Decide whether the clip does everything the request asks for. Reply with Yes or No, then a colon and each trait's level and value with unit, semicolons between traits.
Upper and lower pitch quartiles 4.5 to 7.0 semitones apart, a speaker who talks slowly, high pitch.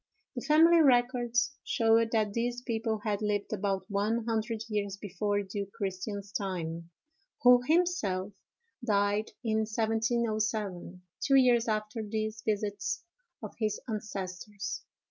No: narrow, 2.5 semitones; slow, 120 wpm; high, 215 Hz